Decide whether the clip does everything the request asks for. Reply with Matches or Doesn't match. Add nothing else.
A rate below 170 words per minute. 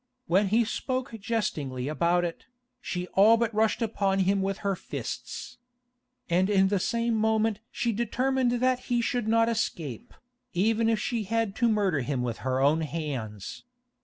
Matches